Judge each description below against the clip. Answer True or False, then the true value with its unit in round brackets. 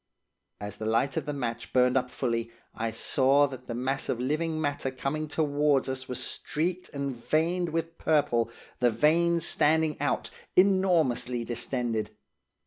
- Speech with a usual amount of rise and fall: True (4.3 semitones)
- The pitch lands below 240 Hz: True (135 Hz)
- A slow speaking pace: False (150 wpm)